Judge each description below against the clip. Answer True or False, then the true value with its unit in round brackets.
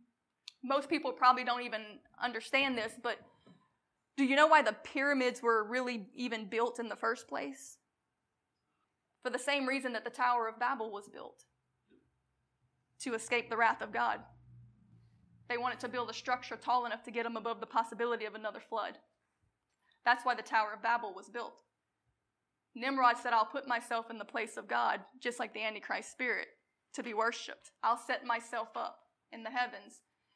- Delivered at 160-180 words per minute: True (175 wpm)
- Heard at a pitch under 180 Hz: False (235 Hz)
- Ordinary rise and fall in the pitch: False (2.0 semitones)